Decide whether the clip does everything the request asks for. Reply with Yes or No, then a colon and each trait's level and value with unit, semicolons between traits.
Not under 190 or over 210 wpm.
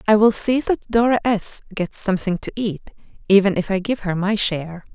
Yes: fast, 205 wpm